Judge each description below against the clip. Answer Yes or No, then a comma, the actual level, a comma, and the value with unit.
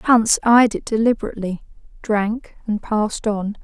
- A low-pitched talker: No, high, 220 Hz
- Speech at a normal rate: No, slow, 130 wpm